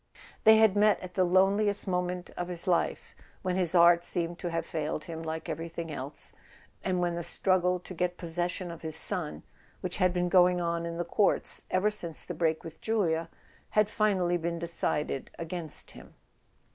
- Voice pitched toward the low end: No, medium, 175 Hz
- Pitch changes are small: Yes, narrow, 1.8 semitones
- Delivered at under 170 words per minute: No, average, 185 wpm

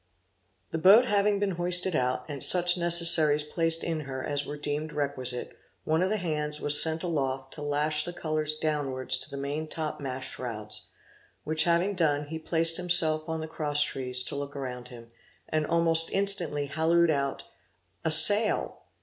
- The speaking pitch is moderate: Yes, medium, 155 Hz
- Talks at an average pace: Yes, average, 170 wpm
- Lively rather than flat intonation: No, average, 2.9 semitones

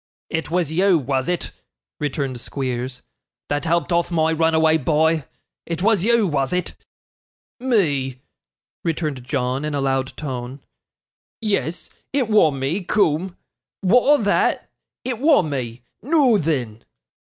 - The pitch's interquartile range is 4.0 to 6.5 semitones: Yes, wide, 5.6 semitones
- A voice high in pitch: No, medium, 160 Hz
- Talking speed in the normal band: No, slow, 130 wpm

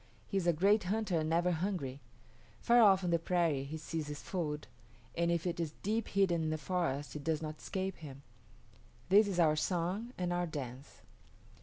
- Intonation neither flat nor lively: Yes, average, 3.6 semitones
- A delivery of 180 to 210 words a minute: Yes, average, 195 wpm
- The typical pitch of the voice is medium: Yes, medium, 170 Hz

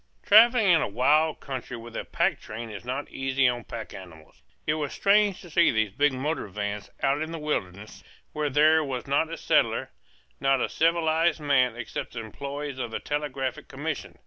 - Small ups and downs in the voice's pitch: No, average, 4.8 semitones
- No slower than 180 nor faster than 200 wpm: Yes, average, 195 wpm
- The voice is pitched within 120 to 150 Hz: Yes, medium, 140 Hz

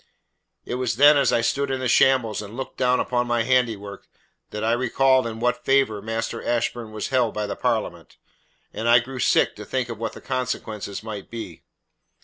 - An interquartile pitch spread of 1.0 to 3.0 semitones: Yes, average, 2.7 semitones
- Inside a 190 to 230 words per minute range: Yes, average, 195 wpm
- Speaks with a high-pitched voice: No, low, 120 Hz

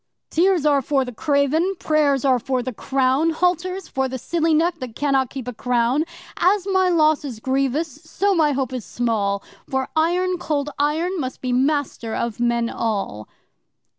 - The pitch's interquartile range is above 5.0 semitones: No, average, 4.5 semitones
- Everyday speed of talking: Yes, average, 170 wpm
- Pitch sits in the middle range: No, very high, 280 Hz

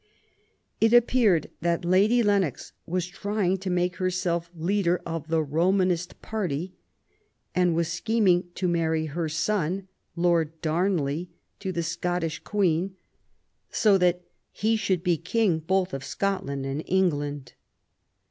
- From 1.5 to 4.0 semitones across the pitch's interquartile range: Yes, average, 2.8 semitones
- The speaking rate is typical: No, slow, 130 wpm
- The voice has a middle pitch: Yes, medium, 180 Hz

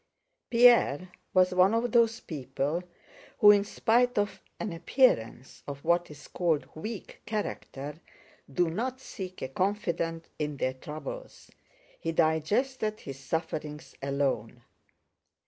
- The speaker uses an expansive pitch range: Yes, wide, 6.5 semitones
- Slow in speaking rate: Yes, slow, 120 wpm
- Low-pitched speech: No, medium, 170 Hz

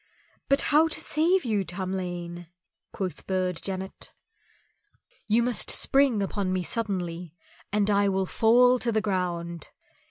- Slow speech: Yes, slow, 130 wpm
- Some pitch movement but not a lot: Yes, average, 4.2 semitones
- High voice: Yes, high, 195 Hz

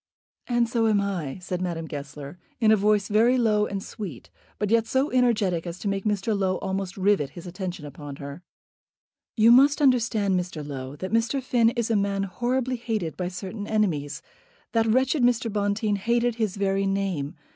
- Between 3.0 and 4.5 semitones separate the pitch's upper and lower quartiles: Yes, average, 4.2 semitones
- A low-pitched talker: No, high, 200 Hz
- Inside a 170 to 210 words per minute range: Yes, average, 180 wpm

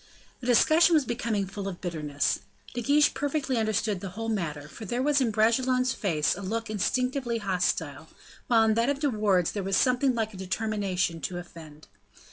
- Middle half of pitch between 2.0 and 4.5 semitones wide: No, wide, 5.5 semitones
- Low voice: No, high, 215 Hz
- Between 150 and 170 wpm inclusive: No, average, 185 wpm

